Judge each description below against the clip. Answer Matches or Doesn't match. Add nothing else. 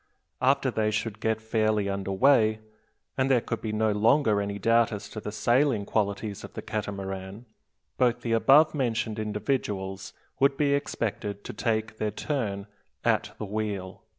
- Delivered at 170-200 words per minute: Doesn't match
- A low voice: Matches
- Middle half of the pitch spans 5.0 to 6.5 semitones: Doesn't match